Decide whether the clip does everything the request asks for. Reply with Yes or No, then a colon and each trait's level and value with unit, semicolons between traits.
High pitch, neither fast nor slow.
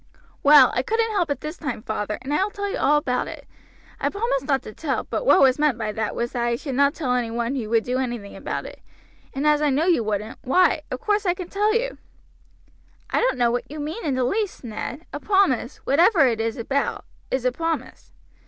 No: very high, 275 Hz; fast, 235 wpm